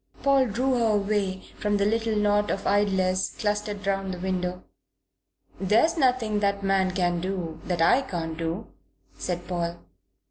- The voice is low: No, high, 195 Hz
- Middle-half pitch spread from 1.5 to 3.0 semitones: Yes, narrow, 2.5 semitones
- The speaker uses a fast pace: No, average, 150 wpm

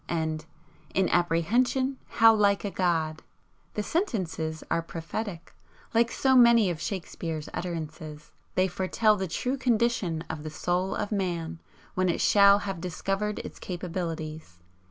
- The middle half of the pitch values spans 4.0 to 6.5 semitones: Yes, average, 4.4 semitones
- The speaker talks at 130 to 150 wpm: Yes, slow, 135 wpm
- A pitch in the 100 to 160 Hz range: No, medium, 185 Hz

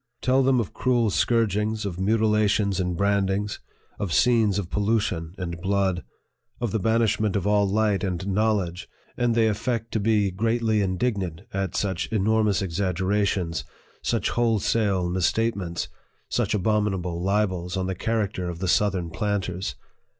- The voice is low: Yes, low, 100 Hz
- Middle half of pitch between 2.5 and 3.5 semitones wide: Yes, average, 2.9 semitones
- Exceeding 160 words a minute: No, average, 145 wpm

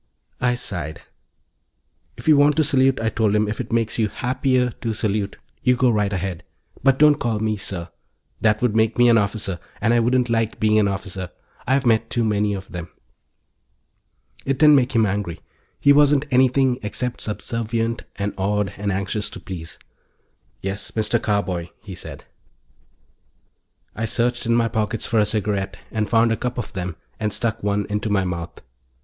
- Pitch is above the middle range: No, low, 110 Hz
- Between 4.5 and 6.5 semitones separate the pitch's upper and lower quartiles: No, average, 3.2 semitones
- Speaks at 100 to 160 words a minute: No, average, 180 wpm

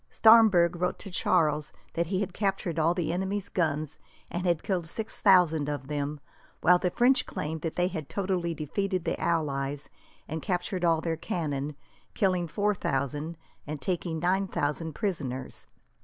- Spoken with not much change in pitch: No, average, 3.5 semitones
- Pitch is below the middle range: No, medium, 170 Hz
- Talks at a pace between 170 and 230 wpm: No, average, 160 wpm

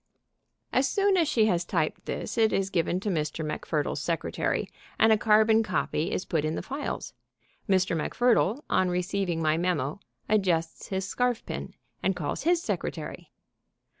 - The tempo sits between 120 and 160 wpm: Yes, average, 155 wpm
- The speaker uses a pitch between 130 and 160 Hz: No, high, 190 Hz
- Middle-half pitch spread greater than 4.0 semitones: Yes, average, 5.1 semitones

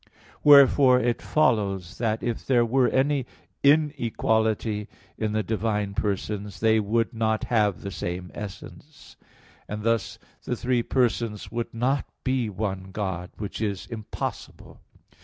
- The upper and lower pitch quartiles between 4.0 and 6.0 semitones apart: No, average, 3.0 semitones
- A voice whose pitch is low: Yes, low, 110 Hz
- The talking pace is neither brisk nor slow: No, slow, 130 wpm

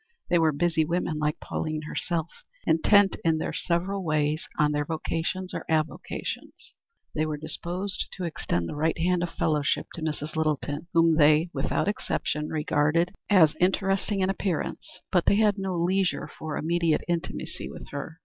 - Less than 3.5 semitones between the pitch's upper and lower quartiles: Yes, average, 2.9 semitones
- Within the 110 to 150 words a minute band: No, average, 160 wpm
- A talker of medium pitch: Yes, medium, 165 Hz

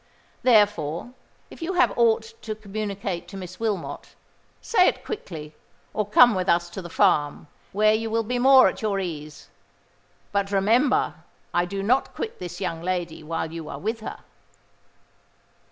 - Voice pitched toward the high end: Yes, high, 200 Hz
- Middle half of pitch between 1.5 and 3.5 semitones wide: No, average, 4.6 semitones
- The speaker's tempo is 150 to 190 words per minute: Yes, average, 155 wpm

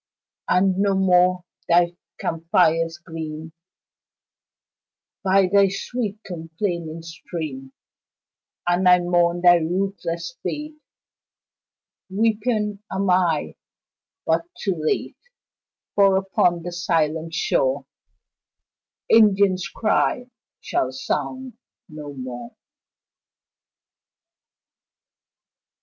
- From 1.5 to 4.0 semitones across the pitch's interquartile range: Yes, average, 3.1 semitones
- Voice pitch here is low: No, medium, 180 Hz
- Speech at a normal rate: No, slow, 80 wpm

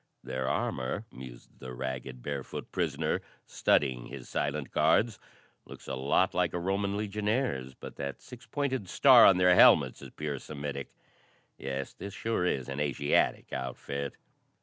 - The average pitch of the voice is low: Yes, very low, 70 Hz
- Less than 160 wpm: Yes, average, 150 wpm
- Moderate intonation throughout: No, wide, 6.9 semitones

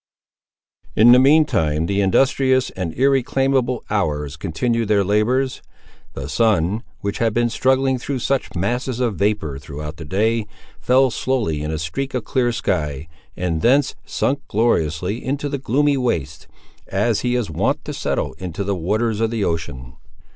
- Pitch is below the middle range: Yes, low, 110 Hz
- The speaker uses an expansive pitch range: Yes, wide, 7.2 semitones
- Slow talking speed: No, average, 160 wpm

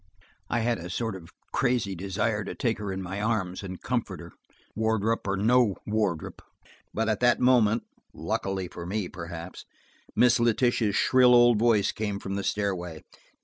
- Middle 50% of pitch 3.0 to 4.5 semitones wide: Yes, average, 3.6 semitones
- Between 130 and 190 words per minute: Yes, average, 165 wpm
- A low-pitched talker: Yes, low, 105 Hz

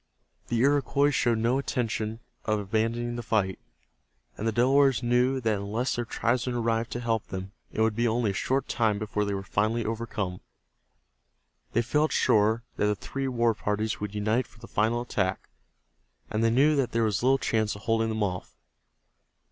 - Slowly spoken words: No, average, 180 wpm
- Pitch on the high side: No, low, 115 Hz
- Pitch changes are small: Yes, narrow, 2.3 semitones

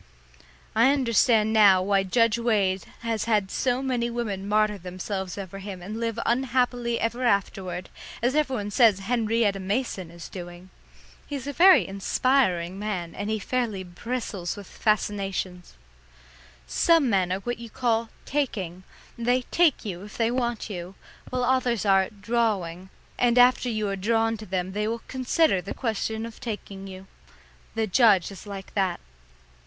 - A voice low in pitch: No, high, 215 Hz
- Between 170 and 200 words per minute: No, average, 155 wpm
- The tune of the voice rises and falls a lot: No, average, 3.8 semitones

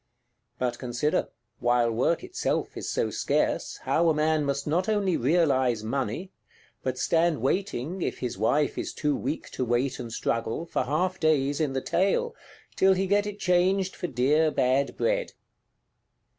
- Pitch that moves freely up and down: Yes, wide, 6.0 semitones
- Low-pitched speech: No, medium, 150 Hz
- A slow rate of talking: No, average, 160 wpm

